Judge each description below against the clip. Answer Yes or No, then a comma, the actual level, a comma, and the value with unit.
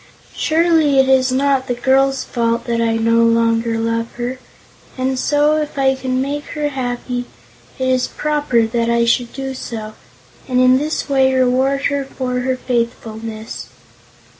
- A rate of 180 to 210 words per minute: No, average, 160 wpm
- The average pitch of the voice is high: Yes, very high, 255 Hz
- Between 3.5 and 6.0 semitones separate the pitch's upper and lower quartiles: No, narrow, 2.6 semitones